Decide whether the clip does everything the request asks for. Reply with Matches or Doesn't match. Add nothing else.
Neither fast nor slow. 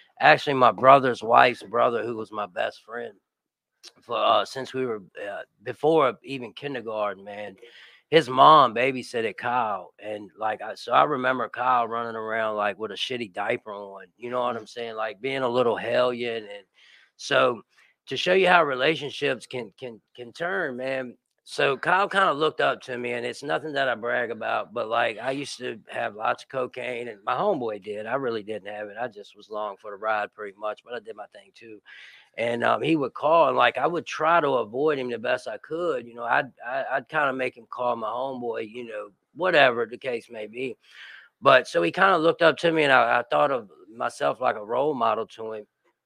Doesn't match